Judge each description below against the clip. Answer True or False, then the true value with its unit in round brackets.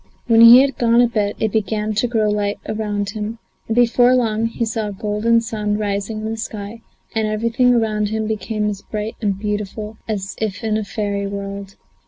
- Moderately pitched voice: False (215 Hz)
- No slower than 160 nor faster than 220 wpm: True (200 wpm)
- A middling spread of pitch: False (1.6 semitones)